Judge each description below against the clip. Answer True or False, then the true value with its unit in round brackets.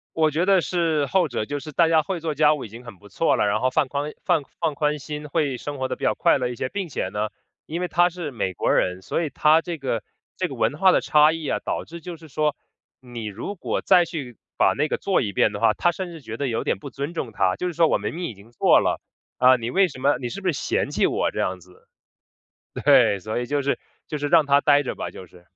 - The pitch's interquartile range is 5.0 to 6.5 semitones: True (5.4 semitones)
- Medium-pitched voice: True (145 Hz)